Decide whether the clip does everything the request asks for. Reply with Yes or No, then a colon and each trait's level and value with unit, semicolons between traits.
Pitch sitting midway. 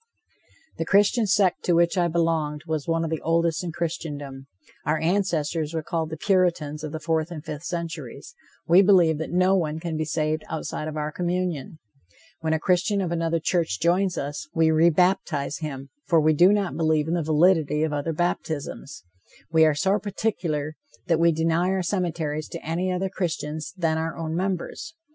Yes: medium, 165 Hz